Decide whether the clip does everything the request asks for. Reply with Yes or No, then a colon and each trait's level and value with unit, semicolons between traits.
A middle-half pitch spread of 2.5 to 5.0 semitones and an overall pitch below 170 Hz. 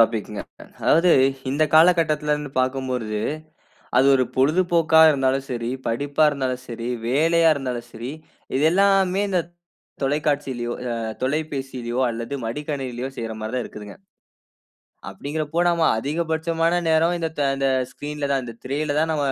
Yes: average, 4.1 semitones; medium, 140 Hz